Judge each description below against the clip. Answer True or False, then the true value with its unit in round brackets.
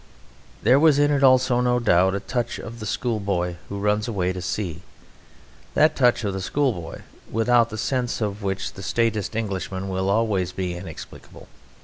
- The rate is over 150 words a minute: True (170 wpm)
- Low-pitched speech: True (105 Hz)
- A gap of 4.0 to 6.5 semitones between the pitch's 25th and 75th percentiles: True (4.4 semitones)